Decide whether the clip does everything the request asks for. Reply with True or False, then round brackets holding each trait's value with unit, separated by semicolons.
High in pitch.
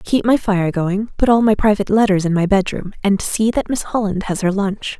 True (200 Hz)